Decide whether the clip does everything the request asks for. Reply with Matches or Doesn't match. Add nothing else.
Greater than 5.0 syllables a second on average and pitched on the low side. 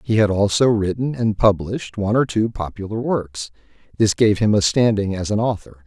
Matches